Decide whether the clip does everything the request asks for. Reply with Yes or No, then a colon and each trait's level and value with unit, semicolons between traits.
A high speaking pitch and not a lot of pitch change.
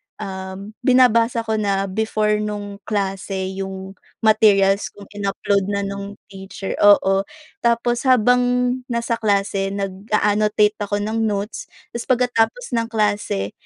Yes: high, 205 Hz; narrow, 2.2 semitones